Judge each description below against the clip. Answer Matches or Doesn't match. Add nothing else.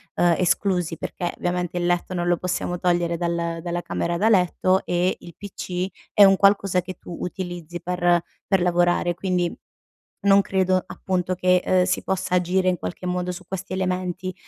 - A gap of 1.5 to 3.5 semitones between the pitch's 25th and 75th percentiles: Doesn't match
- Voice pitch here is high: Doesn't match